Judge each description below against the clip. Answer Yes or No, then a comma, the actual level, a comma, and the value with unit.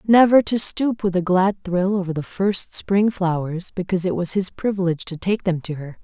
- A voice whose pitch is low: No, medium, 185 Hz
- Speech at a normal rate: No, fast, 220 wpm